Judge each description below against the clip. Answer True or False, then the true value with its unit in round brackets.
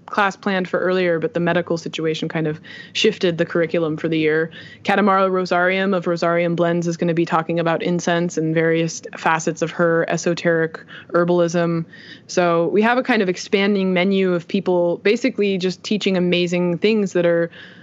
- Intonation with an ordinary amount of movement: False (2.1 semitones)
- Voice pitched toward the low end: False (175 Hz)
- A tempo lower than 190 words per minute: True (175 wpm)